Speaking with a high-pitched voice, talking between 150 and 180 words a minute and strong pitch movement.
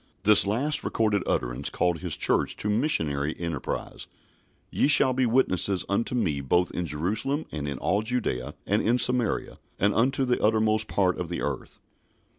No: low, 105 Hz; average, 165 wpm; wide, 6.4 semitones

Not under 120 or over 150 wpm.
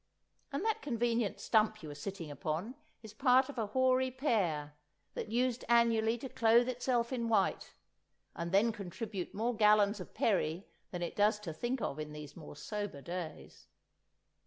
No: average, 160 wpm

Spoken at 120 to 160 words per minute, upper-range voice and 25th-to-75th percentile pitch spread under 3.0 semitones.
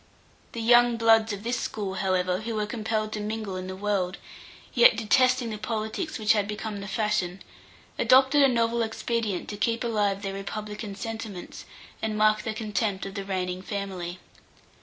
No: average, 170 wpm; high, 215 Hz; narrow, 2.5 semitones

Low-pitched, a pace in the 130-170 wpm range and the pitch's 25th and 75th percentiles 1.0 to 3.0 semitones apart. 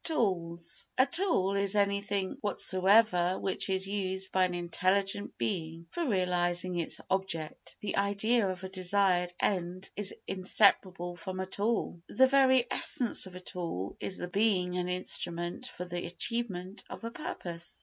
No: high, 190 Hz; average, 150 wpm; narrow, 2.4 semitones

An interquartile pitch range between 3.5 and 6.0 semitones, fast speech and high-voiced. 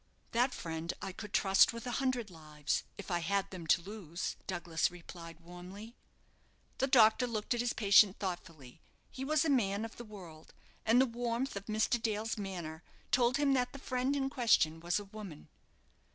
No: wide, 5.6 semitones; average, 180 wpm; high, 205 Hz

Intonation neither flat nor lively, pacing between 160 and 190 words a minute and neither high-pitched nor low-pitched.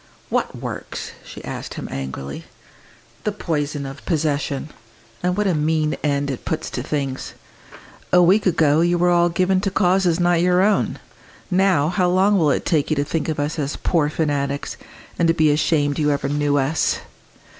Yes: average, 3.7 semitones; average, 180 wpm; medium, 160 Hz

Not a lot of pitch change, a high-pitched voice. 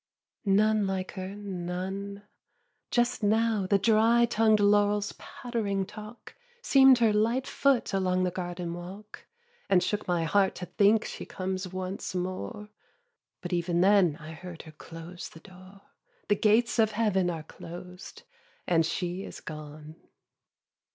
No: average, 3.1 semitones; high, 195 Hz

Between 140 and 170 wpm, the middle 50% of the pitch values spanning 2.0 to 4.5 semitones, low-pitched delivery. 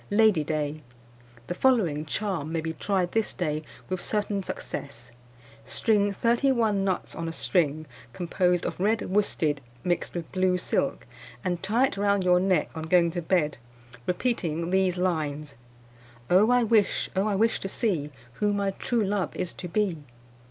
No: average, 165 wpm; average, 4.1 semitones; medium, 185 Hz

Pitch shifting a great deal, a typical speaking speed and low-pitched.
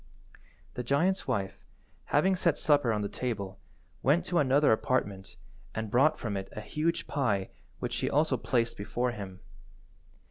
Yes: wide, 6.3 semitones; average, 150 wpm; low, 125 Hz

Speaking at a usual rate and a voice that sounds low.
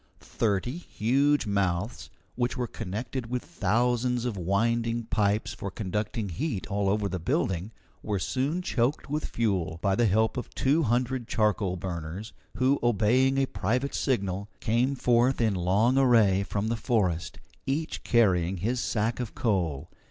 Yes: average, 150 wpm; low, 110 Hz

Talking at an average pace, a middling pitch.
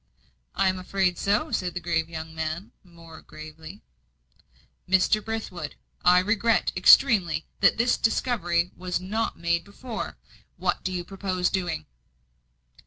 No: slow, 130 wpm; medium, 180 Hz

